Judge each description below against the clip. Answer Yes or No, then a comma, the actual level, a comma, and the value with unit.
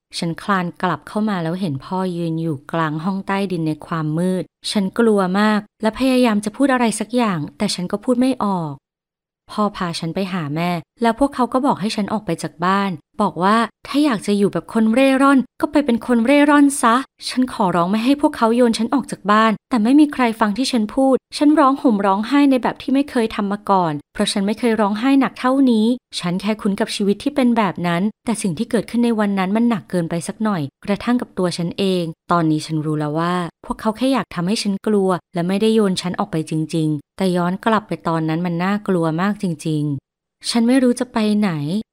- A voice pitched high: Yes, high, 205 Hz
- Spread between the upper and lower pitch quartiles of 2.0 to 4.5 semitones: No, average, 5.2 semitones